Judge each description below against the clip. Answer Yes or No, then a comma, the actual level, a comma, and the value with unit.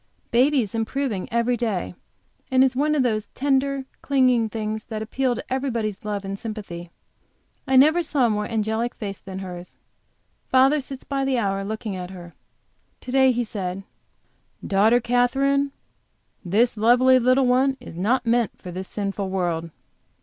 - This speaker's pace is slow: No, average, 165 wpm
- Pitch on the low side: No, high, 235 Hz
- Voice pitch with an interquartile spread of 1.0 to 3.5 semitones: No, average, 4.6 semitones